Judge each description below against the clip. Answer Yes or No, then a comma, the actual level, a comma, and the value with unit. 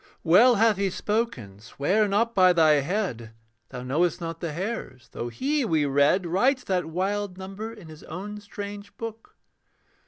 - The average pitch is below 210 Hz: Yes, high, 190 Hz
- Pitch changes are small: No, average, 5.1 semitones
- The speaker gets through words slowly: No, average, 160 wpm